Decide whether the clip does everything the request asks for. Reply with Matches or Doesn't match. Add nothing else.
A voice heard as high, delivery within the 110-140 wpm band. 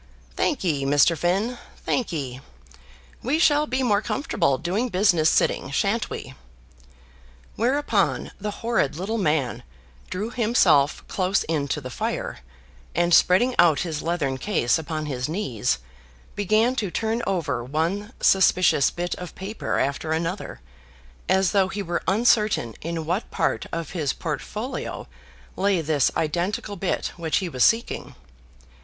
Doesn't match